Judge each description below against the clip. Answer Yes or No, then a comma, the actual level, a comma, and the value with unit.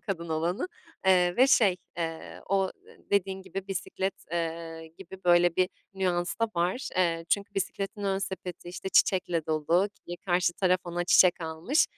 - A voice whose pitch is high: No, medium, 180 Hz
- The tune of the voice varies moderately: No, narrow, 2.1 semitones